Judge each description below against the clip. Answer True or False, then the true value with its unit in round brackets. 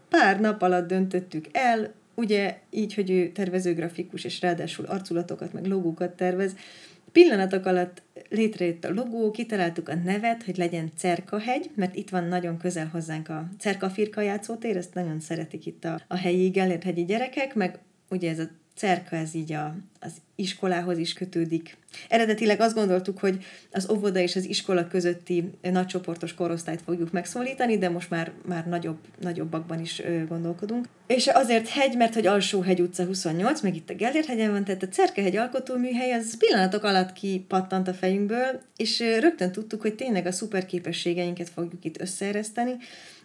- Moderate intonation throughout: True (3.1 semitones)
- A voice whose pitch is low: False (185 Hz)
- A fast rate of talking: True (160 wpm)